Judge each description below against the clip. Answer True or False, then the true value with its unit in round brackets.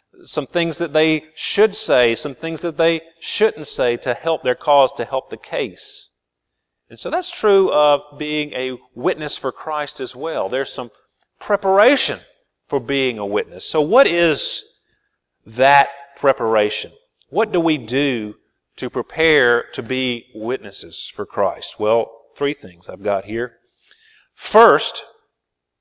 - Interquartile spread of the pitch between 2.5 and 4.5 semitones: False (5.2 semitones)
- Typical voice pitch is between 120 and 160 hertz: True (140 Hz)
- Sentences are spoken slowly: False (145 wpm)